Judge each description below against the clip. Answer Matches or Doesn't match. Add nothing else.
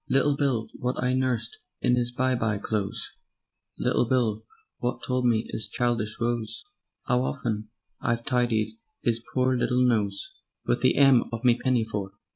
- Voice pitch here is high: Doesn't match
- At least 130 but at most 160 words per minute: Matches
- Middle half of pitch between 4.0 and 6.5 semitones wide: Doesn't match